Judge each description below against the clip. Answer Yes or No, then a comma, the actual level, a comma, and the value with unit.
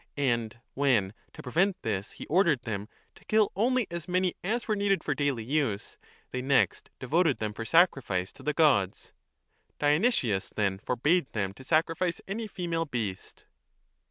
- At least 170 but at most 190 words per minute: No, average, 155 wpm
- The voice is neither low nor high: Yes, medium, 145 Hz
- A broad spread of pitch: Yes, wide, 8.1 semitones